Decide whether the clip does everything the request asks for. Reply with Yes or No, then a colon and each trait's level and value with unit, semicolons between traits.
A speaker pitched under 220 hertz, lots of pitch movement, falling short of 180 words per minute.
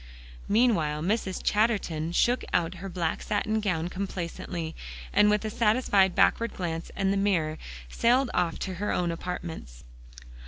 No: high, 190 Hz; average, 3.9 semitones; average, 145 wpm